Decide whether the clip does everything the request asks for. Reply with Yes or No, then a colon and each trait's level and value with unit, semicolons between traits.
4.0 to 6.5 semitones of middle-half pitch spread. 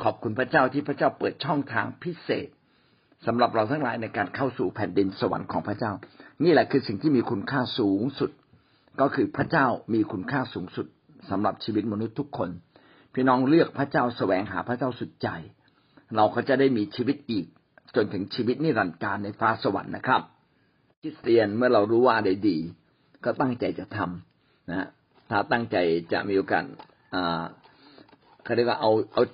Yes: average, 4.4 semitones